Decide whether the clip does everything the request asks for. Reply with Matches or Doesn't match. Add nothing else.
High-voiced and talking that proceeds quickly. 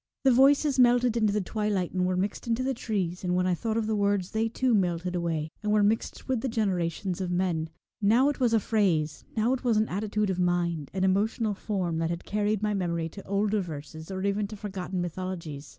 Matches